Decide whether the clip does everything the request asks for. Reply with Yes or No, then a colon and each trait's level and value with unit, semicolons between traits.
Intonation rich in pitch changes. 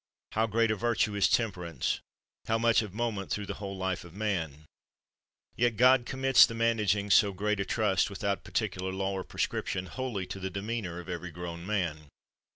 No: average, 3.4 semitones